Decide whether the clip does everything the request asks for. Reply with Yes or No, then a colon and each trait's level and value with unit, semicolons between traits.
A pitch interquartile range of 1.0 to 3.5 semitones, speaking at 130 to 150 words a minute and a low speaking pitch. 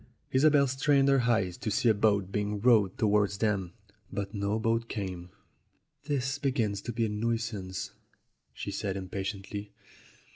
Yes: average, 3.1 semitones; average, 145 wpm; low, 105 Hz